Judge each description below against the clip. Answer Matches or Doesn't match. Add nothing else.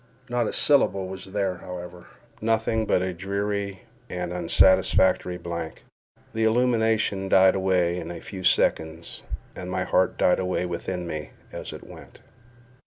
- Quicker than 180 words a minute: Doesn't match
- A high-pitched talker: Doesn't match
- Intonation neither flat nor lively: Doesn't match